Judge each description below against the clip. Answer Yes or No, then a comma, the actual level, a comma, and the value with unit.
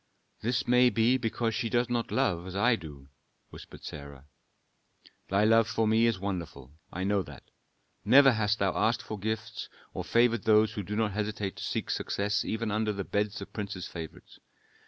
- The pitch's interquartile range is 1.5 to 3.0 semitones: Yes, average, 2.7 semitones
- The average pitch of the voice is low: Yes, low, 105 Hz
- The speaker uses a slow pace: No, average, 180 wpm